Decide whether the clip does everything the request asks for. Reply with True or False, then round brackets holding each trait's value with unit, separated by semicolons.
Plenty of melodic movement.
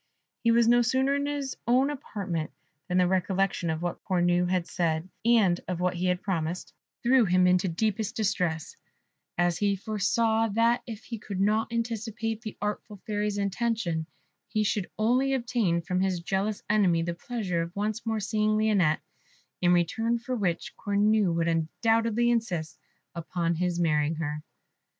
False (4.3 semitones)